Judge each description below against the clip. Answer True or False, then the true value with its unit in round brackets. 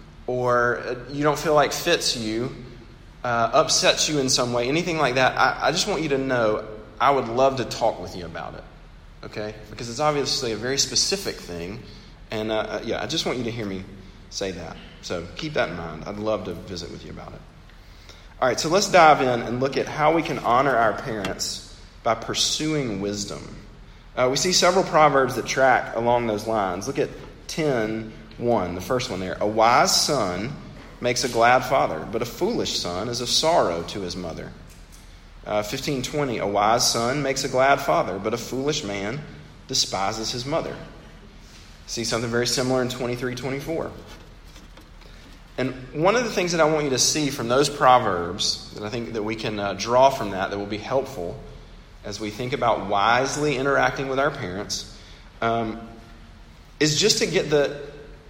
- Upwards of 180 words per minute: True (190 wpm)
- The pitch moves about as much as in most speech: True (4.9 semitones)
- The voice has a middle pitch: False (120 Hz)